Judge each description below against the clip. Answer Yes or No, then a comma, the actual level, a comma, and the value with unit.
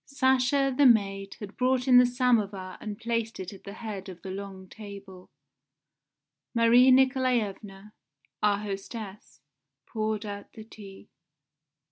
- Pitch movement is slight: No, average, 4.0 semitones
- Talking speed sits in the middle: No, slow, 130 wpm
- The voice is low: No, high, 210 Hz